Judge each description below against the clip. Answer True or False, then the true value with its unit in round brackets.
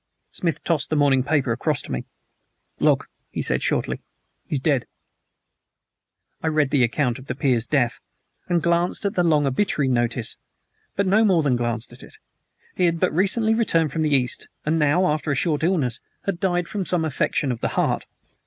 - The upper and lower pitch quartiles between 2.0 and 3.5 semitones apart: False (5.0 semitones)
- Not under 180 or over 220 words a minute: True (190 wpm)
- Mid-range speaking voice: True (150 Hz)